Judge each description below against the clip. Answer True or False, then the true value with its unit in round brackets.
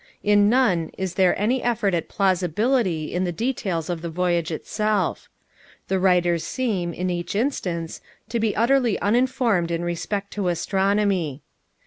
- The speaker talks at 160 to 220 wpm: False (145 wpm)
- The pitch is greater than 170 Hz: True (190 Hz)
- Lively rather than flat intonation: False (3.8 semitones)